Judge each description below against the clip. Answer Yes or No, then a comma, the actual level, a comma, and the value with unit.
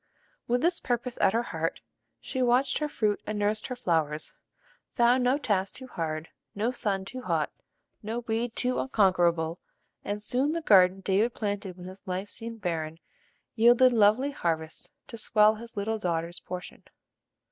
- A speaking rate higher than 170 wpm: No, average, 160 wpm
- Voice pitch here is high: Yes, high, 215 Hz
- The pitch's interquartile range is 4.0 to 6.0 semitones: Yes, average, 4.8 semitones